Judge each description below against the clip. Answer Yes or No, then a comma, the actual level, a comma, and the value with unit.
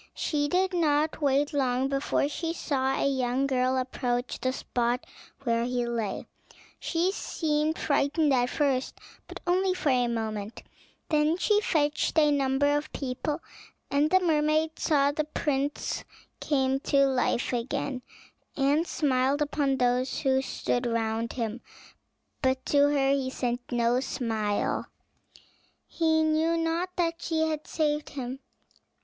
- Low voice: No, very high, 275 Hz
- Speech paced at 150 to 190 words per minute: No, average, 140 wpm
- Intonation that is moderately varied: Yes, average, 3.4 semitones